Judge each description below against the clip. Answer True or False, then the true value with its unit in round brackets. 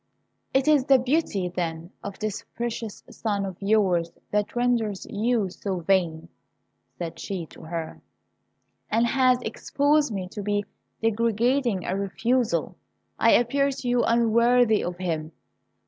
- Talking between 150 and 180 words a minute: False (135 wpm)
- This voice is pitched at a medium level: False (215 Hz)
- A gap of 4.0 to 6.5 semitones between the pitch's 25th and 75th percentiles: True (4.6 semitones)